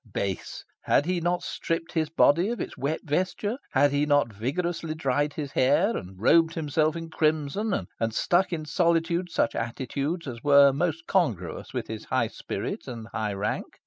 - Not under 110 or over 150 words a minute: No, average, 175 wpm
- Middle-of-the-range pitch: Yes, medium, 155 Hz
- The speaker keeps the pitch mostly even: No, average, 4.2 semitones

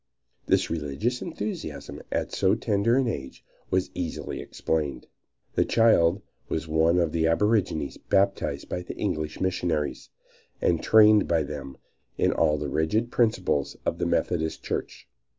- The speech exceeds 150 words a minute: No, average, 140 wpm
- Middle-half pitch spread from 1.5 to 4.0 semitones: No, average, 5.3 semitones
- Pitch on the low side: Yes, very low, 85 Hz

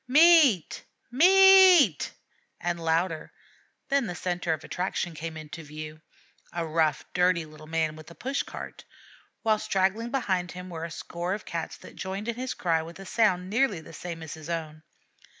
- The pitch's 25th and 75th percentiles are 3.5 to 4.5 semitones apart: No, average, 5.2 semitones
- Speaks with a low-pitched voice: No, medium, 175 Hz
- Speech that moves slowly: No, average, 170 wpm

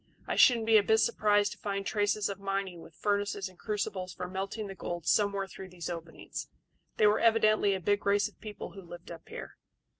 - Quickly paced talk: Yes, fast, 210 wpm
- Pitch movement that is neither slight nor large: No, narrow, 2.0 semitones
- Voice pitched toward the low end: No, high, 200 Hz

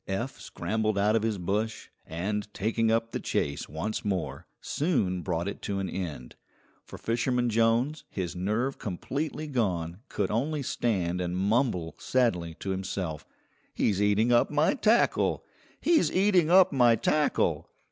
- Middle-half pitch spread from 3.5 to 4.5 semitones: No, average, 5.1 semitones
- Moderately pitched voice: No, low, 105 Hz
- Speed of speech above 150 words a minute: No, average, 145 wpm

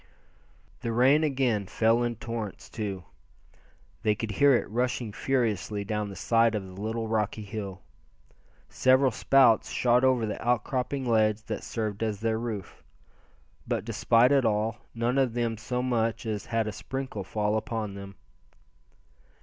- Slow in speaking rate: No, average, 150 wpm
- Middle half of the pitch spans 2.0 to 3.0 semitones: Yes, narrow, 2.5 semitones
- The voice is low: Yes, low, 115 Hz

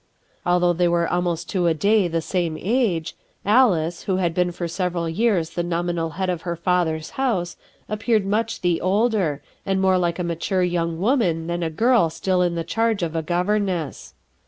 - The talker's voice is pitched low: No, medium, 175 Hz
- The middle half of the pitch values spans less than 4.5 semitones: Yes, average, 2.7 semitones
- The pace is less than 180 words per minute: No, average, 190 wpm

